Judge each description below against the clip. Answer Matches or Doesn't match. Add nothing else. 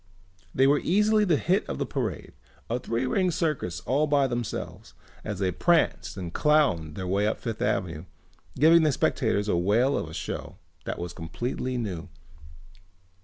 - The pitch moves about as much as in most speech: Doesn't match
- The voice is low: Matches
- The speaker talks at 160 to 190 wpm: Matches